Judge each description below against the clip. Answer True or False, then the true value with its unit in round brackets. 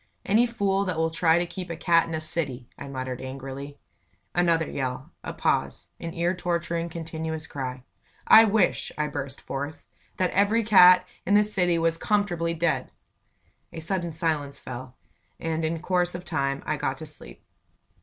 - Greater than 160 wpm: True (170 wpm)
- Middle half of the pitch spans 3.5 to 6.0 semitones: True (3.9 semitones)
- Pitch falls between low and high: True (165 Hz)